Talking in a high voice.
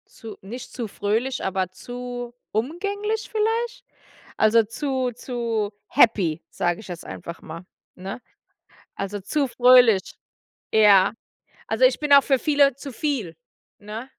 Yes: high, 240 Hz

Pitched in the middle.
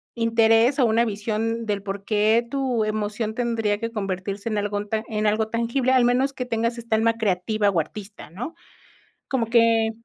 No: high, 225 Hz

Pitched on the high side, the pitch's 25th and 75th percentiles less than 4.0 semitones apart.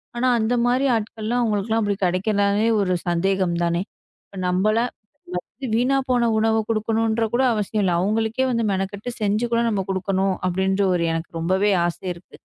Yes: high, 210 Hz; average, 3.0 semitones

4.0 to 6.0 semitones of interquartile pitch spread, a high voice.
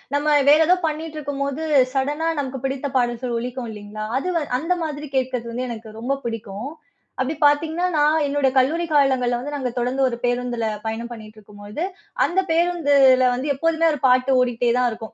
No: average, 3.6 semitones; very high, 260 Hz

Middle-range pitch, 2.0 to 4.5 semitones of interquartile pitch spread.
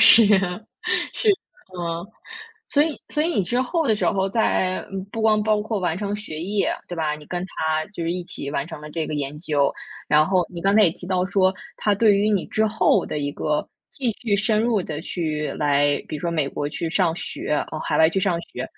No: medium, 180 Hz; average, 5.1 semitones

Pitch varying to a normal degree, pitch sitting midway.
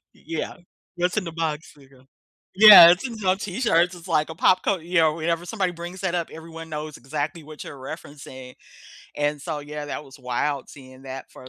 Yes: average, 3.3 semitones; medium, 160 Hz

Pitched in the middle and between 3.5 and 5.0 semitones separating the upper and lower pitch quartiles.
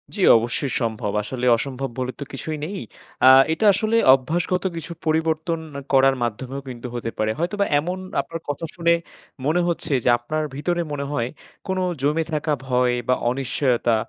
Yes: medium, 145 Hz; average, 4.7 semitones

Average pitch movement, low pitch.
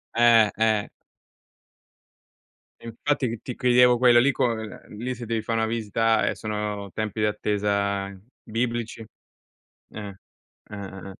No: narrow, 2.2 semitones; low, 110 Hz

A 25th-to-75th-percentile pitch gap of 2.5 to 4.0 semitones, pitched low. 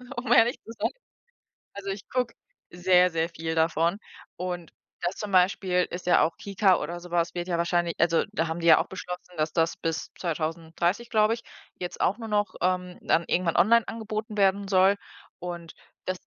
No: average, 2.9 semitones; medium, 180 Hz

